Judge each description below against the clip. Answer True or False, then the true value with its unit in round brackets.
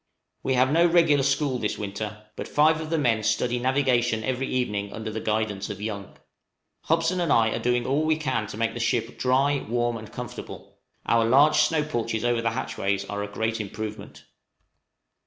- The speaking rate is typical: True (190 wpm)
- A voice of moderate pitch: False (120 Hz)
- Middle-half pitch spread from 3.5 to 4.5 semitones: True (4.0 semitones)